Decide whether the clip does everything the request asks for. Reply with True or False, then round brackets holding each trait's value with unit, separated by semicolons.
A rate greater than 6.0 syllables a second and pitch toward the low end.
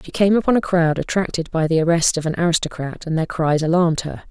False (6.3 syllables/s; 165 Hz)